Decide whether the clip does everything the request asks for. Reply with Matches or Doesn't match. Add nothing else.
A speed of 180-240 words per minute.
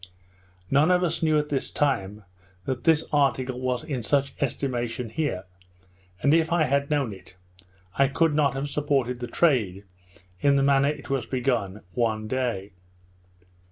Doesn't match